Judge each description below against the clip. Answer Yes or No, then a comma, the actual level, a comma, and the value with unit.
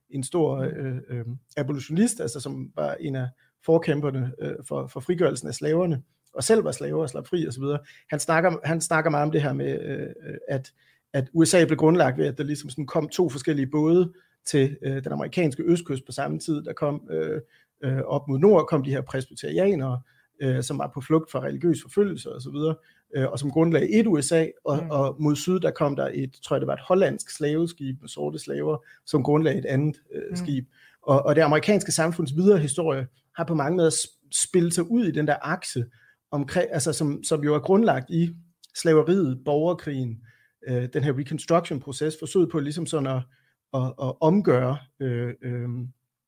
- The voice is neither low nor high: Yes, medium, 150 Hz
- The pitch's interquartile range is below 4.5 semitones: Yes, average, 3.5 semitones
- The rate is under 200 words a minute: Yes, average, 190 wpm